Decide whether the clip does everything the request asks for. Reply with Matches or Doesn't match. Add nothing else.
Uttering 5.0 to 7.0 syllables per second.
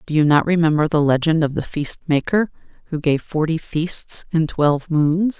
Doesn't match